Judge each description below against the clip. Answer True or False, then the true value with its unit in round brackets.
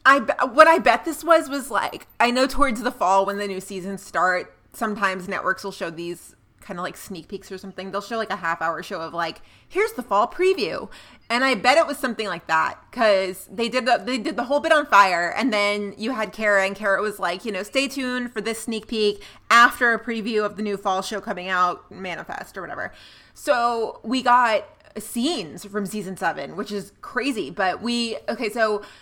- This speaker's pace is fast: True (220 wpm)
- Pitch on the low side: False (215 Hz)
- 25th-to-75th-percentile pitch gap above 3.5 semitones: True (4.6 semitones)